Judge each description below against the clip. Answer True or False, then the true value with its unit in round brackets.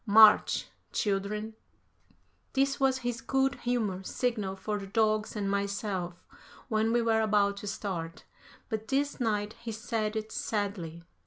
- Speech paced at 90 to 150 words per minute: True (140 wpm)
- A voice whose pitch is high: True (215 Hz)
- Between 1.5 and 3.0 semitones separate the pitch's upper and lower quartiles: True (2.5 semitones)